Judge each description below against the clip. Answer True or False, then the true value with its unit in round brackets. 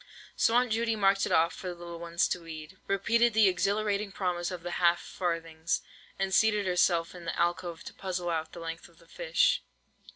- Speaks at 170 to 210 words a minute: True (200 wpm)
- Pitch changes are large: False (2.9 semitones)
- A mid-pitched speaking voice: True (180 Hz)